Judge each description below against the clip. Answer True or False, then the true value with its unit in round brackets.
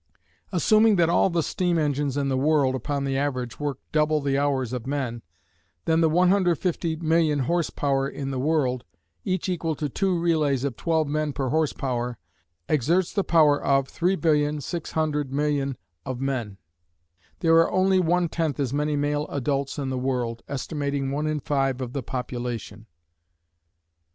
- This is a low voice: False (145 Hz)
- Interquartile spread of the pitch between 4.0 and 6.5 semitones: False (3.2 semitones)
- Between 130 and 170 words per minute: True (155 wpm)